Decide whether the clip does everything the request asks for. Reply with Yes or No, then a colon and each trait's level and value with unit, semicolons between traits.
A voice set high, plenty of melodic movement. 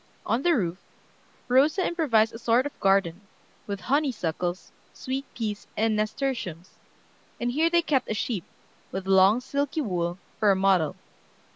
Yes: high, 220 Hz; wide, 6.0 semitones